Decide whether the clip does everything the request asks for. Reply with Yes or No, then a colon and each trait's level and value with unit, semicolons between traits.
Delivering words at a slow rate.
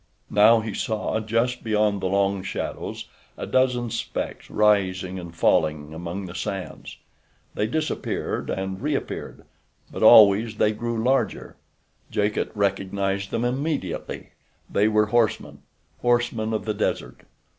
Yes: slow, 125 wpm